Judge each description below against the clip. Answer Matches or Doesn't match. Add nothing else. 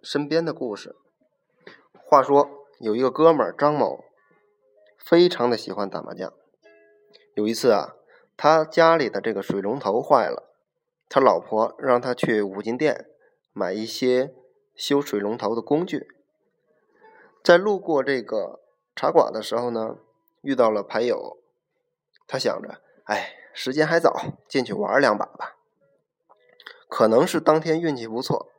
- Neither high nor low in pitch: Matches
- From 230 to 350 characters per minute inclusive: Doesn't match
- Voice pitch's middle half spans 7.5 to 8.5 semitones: Matches